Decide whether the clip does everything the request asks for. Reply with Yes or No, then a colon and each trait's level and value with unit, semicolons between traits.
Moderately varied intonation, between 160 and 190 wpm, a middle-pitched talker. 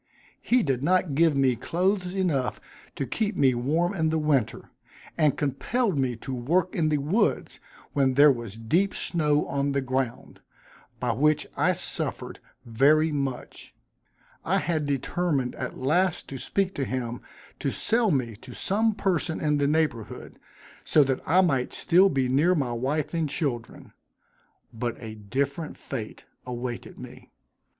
No: average, 4.9 semitones; average, 150 wpm; medium, 145 Hz